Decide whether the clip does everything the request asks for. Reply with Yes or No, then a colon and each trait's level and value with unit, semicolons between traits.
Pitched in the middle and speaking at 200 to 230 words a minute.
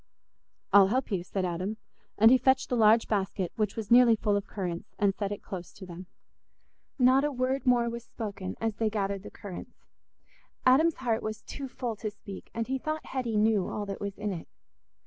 No: high, 215 Hz; fast, 205 wpm